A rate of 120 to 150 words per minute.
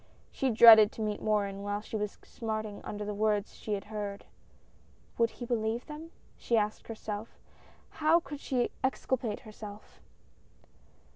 Yes: average, 145 wpm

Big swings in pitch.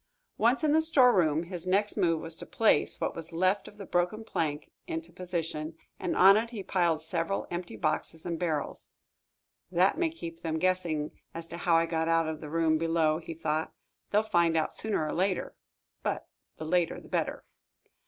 No: average, 2.9 semitones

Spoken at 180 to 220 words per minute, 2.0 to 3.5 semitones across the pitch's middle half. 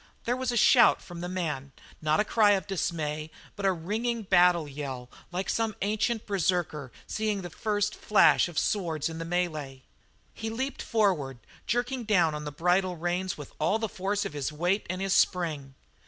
No: average, 185 wpm; average, 5.1 semitones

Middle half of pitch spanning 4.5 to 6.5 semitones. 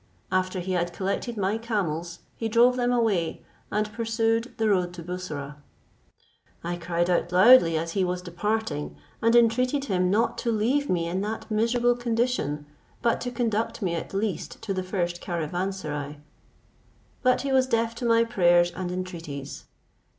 Yes: average, 4.9 semitones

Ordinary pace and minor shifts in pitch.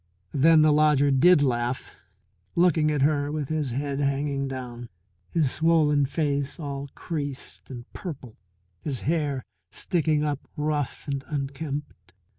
No: slow, 130 wpm; narrow, 1.9 semitones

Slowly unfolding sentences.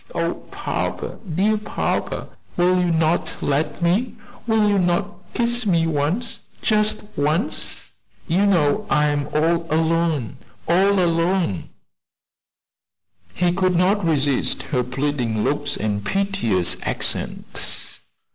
Yes: slow, 115 wpm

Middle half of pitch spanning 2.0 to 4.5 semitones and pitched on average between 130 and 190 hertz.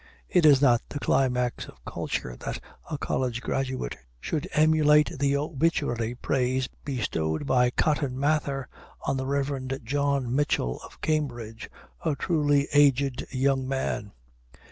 Yes: average, 2.8 semitones; low, 135 Hz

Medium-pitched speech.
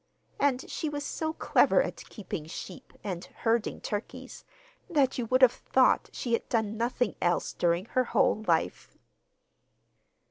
No: high, 235 Hz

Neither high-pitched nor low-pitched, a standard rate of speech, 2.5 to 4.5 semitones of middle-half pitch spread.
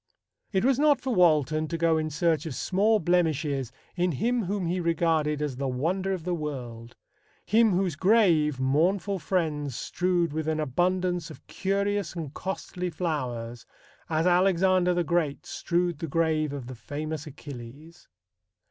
Yes: medium, 165 Hz; average, 155 wpm; average, 3.6 semitones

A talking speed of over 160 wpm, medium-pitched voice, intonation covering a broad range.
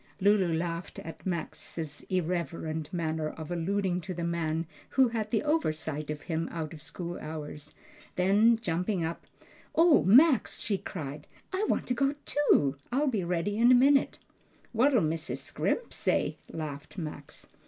No: average, 155 wpm; medium, 175 Hz; wide, 5.7 semitones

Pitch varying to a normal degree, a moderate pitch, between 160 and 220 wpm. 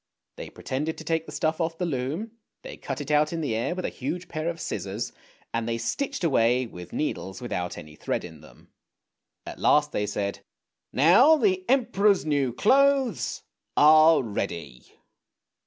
No: wide, 7.5 semitones; medium, 150 Hz; average, 170 wpm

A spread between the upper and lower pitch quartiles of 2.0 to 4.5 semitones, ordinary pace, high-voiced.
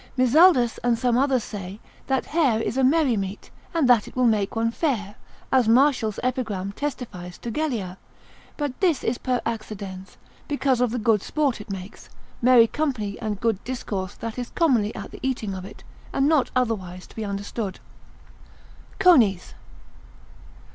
Yes: average, 4.2 semitones; average, 160 wpm; high, 230 Hz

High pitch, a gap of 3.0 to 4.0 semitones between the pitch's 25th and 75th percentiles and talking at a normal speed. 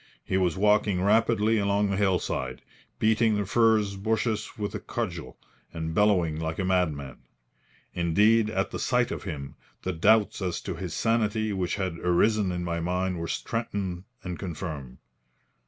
No: very low, 95 Hz; average, 3.7 semitones; average, 155 wpm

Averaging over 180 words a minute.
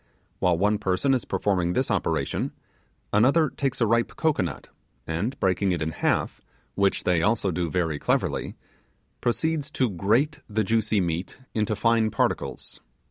No: average, 145 wpm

